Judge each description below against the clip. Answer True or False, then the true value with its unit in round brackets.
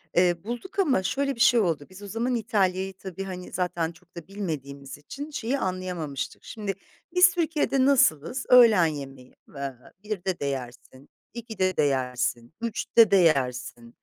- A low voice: False (185 Hz)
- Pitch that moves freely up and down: True (8.0 semitones)